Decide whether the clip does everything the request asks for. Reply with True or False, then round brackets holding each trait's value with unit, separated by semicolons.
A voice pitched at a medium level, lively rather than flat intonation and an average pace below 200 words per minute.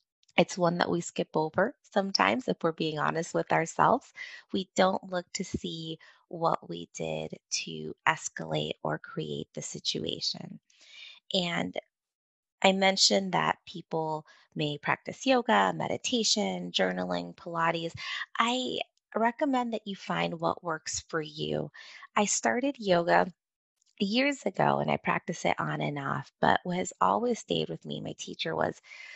True (180 Hz; 5.9 semitones; 140 wpm)